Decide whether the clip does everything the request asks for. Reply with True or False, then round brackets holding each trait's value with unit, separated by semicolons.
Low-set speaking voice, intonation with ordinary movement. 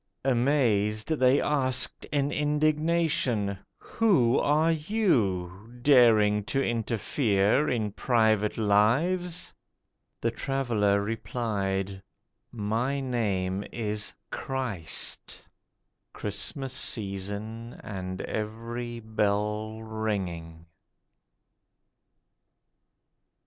True (110 Hz; 4.6 semitones)